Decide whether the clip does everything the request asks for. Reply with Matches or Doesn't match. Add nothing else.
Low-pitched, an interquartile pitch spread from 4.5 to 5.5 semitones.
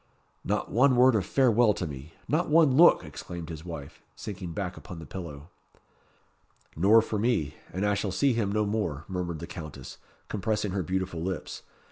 Matches